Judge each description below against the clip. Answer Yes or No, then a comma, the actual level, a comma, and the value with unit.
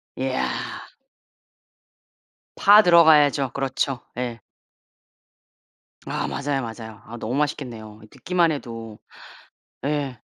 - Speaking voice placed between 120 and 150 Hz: Yes, low, 135 Hz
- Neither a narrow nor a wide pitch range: Yes, average, 4.5 semitones